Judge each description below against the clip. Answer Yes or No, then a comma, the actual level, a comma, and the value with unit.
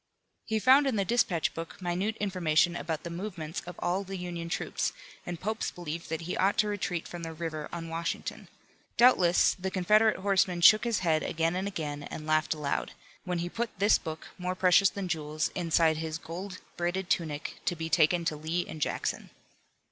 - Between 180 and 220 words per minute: Yes, average, 190 wpm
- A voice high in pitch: No, medium, 175 Hz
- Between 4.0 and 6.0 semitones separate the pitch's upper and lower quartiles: No, average, 2.9 semitones